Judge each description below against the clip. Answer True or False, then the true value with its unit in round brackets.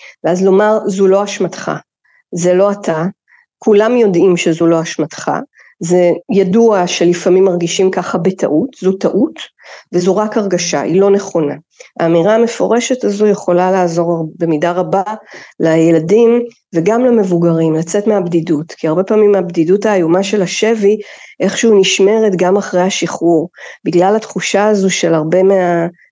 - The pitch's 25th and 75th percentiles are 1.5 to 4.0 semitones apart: True (3.4 semitones)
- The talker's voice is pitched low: False (190 Hz)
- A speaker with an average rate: True (130 wpm)